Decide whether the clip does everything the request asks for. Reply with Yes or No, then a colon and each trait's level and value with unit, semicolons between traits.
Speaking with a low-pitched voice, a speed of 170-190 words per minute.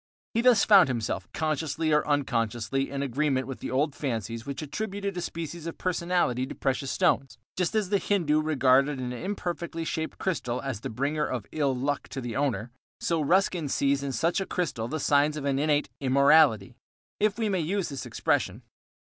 No: medium, 145 Hz; average, 185 wpm